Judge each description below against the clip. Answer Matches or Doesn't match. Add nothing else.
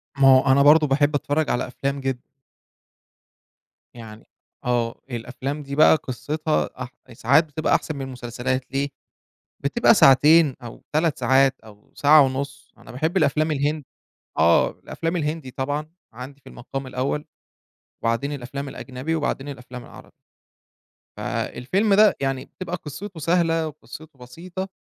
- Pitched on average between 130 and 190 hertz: Matches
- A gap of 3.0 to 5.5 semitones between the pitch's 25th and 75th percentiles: Matches